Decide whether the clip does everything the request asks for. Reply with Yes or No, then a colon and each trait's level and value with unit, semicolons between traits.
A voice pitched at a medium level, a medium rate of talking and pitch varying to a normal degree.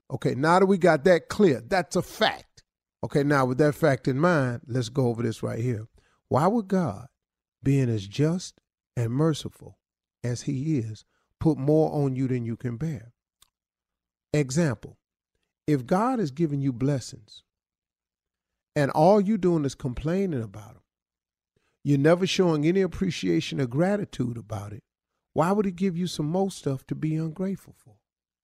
No: medium, 145 Hz; average, 165 wpm; wide, 6.1 semitones